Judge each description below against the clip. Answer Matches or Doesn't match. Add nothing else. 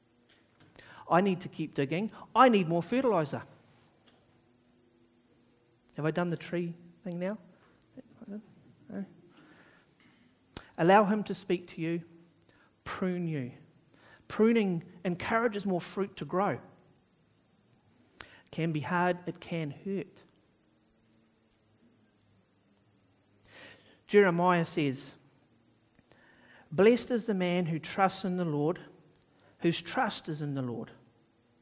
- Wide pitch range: Matches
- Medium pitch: Matches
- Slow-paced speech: Matches